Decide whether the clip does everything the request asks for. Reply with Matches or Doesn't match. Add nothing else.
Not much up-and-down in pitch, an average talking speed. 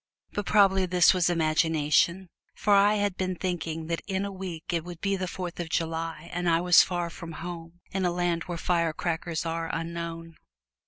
Matches